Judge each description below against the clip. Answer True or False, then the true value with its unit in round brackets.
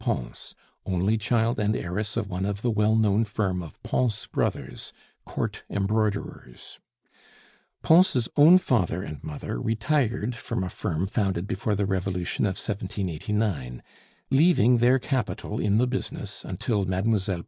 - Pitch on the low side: True (105 Hz)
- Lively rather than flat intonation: False (3.5 semitones)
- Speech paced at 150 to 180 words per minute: False (135 wpm)